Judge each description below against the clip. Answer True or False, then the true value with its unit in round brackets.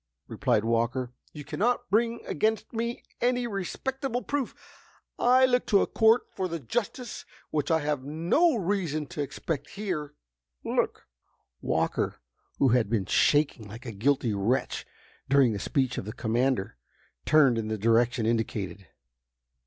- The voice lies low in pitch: False (145 Hz)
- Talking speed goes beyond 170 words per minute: False (145 wpm)